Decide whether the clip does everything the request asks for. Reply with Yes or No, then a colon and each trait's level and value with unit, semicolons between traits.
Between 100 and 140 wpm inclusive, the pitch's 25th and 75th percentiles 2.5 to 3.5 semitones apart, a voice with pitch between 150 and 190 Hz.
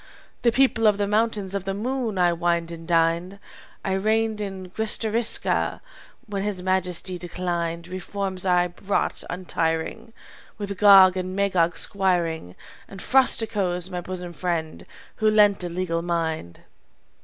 Yes: slow, 135 wpm; average, 2.9 semitones; medium, 185 Hz